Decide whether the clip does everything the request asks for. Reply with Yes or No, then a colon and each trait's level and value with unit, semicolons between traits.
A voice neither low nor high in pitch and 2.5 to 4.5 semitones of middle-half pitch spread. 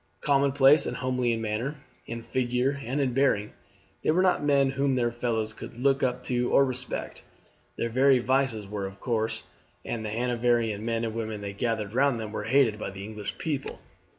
No: low, 120 Hz; average, 3.5 semitones